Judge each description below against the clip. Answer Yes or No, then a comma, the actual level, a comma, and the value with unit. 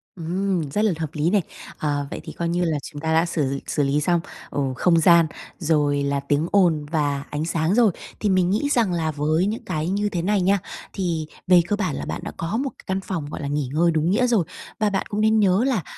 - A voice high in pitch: No, medium, 170 Hz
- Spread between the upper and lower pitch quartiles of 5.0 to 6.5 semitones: No, average, 4.6 semitones